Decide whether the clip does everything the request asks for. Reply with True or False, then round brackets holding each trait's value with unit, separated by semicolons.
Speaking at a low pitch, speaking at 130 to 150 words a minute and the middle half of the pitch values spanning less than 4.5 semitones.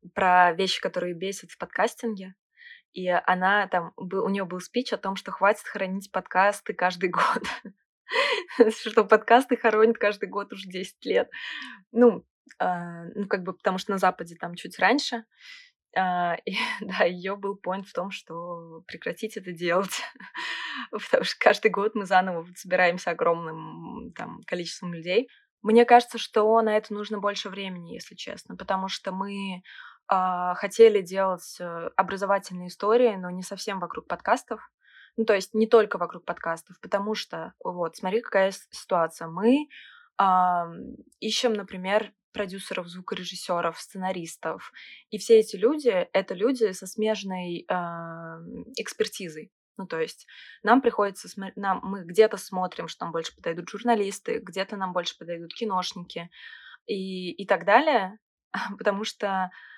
False (195 Hz; 145 wpm; 3.3 semitones)